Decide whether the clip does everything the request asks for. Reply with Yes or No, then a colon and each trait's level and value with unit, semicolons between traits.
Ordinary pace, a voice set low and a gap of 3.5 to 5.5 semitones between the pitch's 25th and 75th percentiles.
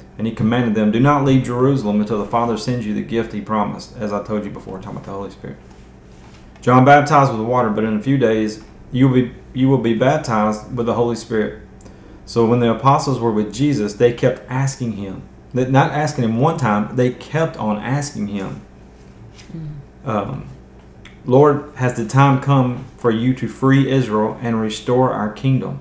Yes: average, 195 wpm; low, 115 Hz; average, 3.8 semitones